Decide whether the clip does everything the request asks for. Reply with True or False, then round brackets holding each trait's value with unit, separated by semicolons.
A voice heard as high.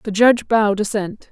True (215 Hz)